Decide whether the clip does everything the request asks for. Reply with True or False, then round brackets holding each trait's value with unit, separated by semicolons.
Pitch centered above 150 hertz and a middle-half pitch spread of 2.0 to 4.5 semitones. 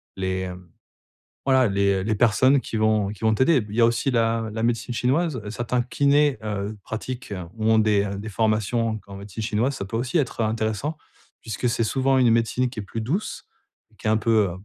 False (115 Hz; 2.9 semitones)